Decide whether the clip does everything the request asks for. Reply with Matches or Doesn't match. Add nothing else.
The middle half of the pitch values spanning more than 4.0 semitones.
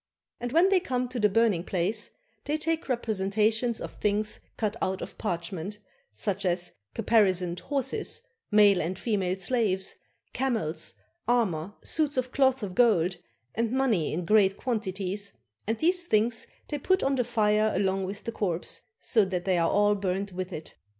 Matches